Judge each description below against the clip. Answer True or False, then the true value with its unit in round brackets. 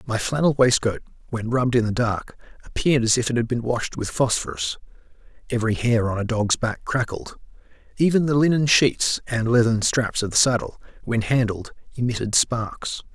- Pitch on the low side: True (120 Hz)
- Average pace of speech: True (165 wpm)